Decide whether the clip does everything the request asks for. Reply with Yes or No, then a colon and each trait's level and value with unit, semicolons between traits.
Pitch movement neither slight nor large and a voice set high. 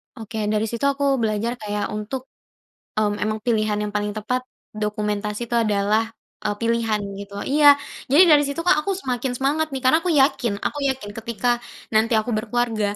Yes: average, 3.7 semitones; high, 225 Hz